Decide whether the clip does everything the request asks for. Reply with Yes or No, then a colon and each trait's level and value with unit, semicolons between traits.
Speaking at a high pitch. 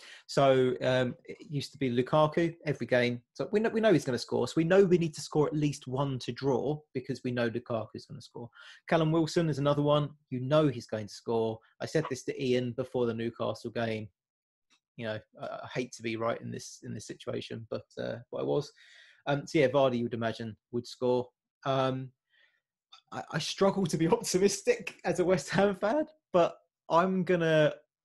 No: low, 135 Hz